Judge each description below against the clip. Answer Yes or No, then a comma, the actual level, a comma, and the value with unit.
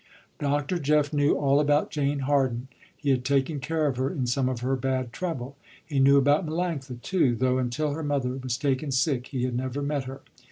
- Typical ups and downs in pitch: No, narrow, 2.2 semitones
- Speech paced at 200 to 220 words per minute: Yes, fast, 205 wpm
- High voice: No, medium, 140 Hz